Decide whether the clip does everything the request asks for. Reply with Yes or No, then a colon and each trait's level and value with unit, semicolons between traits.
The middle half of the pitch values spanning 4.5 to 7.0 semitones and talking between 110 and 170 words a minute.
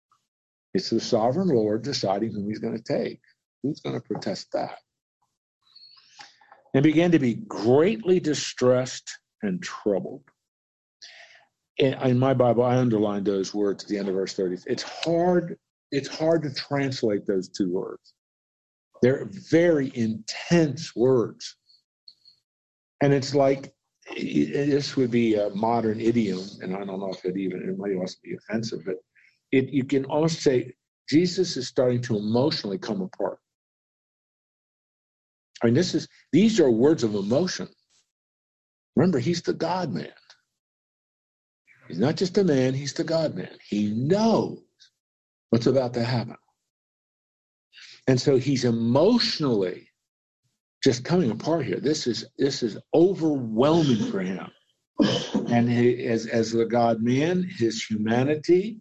Yes: average, 5.2 semitones; average, 140 wpm